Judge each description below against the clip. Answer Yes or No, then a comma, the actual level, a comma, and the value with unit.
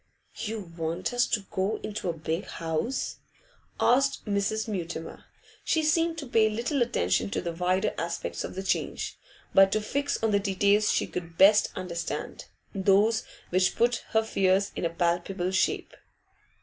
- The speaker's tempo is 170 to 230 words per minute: No, average, 155 wpm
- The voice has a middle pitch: No, high, 195 Hz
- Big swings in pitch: No, average, 4.0 semitones